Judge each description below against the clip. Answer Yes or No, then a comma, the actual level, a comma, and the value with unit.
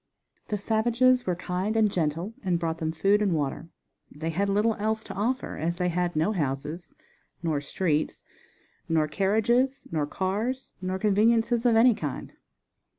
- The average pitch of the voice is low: No, high, 190 Hz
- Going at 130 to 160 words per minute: Yes, average, 155 wpm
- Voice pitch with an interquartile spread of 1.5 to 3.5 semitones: No, average, 5.2 semitones